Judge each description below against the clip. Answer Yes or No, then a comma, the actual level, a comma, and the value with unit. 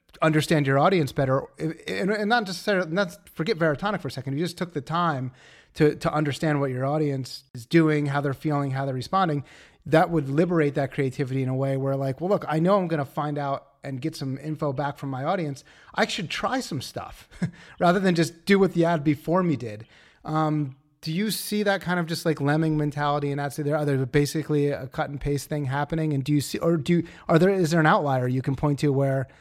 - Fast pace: Yes, fast, 235 wpm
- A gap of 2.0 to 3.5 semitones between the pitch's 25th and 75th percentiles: Yes, average, 3.2 semitones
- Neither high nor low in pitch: Yes, medium, 150 Hz